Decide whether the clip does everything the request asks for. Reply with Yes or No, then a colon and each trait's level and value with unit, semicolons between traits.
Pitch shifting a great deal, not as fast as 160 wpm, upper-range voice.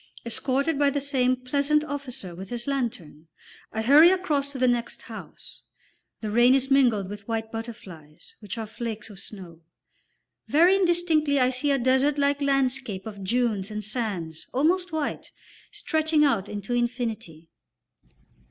No: average, 4.9 semitones; average, 150 wpm; very high, 250 Hz